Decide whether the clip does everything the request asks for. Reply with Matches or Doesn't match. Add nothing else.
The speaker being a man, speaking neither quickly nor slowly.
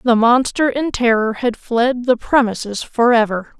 Doesn't match